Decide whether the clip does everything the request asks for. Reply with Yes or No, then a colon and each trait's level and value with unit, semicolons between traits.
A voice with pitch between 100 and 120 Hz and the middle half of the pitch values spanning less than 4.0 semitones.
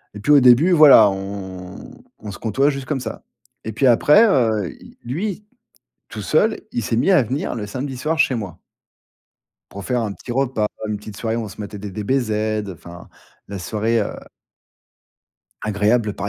No: low, 110 Hz; average, 4.4 semitones